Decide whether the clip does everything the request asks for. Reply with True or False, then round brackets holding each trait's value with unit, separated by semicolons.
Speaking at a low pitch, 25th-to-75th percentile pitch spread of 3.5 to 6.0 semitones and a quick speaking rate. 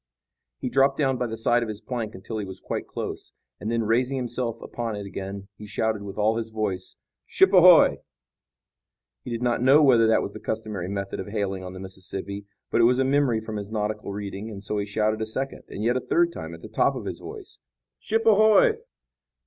True (110 Hz; 3.8 semitones; 220 wpm)